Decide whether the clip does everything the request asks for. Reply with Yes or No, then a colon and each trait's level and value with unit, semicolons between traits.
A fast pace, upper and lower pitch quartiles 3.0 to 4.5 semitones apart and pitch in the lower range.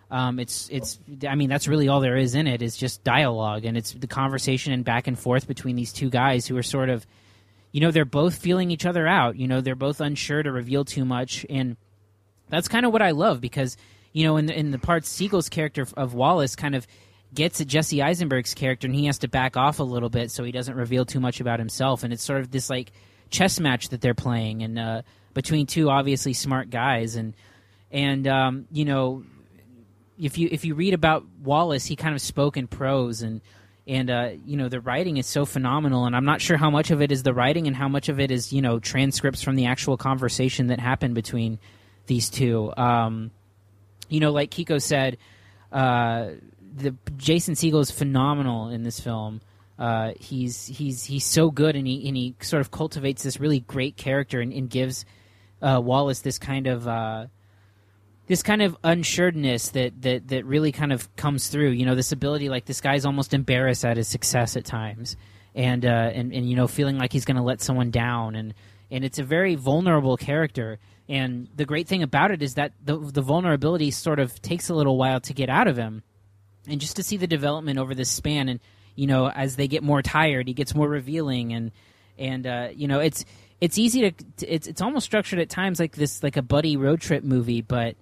Yes: fast, 220 wpm; average, 3.5 semitones; low, 130 Hz